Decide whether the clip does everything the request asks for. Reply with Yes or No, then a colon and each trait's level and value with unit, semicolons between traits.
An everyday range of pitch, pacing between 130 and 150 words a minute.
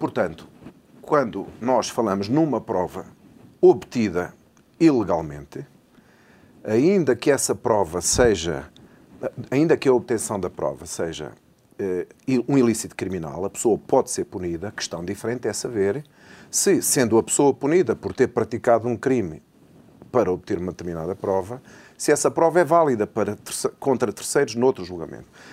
No: wide, 5.8 semitones; average, 135 wpm